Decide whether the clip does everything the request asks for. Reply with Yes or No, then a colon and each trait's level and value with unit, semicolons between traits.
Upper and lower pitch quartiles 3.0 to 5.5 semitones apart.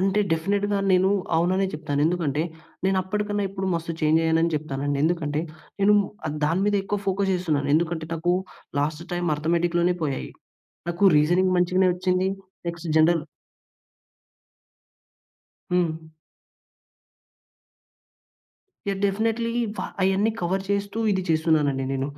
Yes: average, 3.4 semitones